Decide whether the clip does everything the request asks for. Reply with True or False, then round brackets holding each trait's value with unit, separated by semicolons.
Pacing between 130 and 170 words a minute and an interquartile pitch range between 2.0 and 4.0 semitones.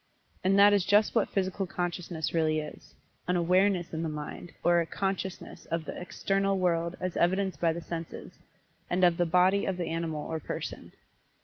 False (185 wpm; 2.4 semitones)